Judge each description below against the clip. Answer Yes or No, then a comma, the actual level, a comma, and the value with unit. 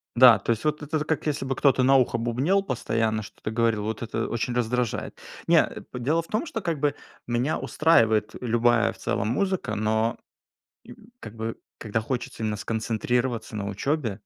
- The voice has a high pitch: No, low, 120 Hz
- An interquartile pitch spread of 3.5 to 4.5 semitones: Yes, average, 3.8 semitones